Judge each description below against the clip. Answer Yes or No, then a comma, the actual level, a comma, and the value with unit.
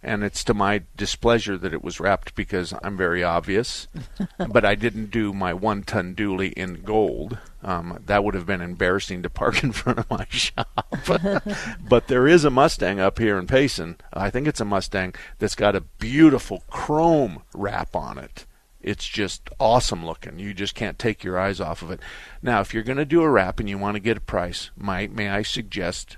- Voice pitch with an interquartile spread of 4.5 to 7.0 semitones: No, average, 3.8 semitones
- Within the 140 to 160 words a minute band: No, fast, 205 wpm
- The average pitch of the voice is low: Yes, low, 100 Hz